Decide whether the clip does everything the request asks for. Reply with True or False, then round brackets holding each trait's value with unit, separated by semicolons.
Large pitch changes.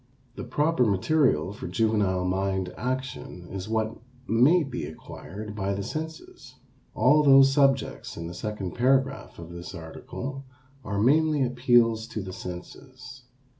True (6.0 semitones)